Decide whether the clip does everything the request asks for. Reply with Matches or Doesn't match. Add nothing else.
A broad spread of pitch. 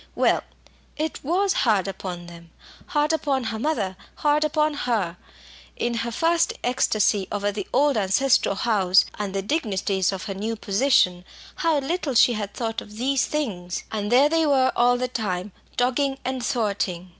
Matches